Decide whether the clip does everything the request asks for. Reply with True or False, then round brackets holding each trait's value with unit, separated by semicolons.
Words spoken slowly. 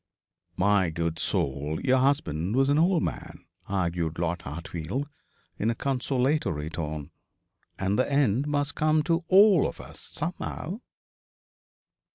True (130 wpm)